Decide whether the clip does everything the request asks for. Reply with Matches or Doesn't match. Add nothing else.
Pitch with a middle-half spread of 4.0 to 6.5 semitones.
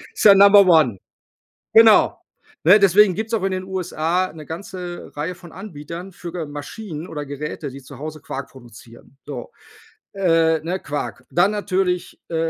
Matches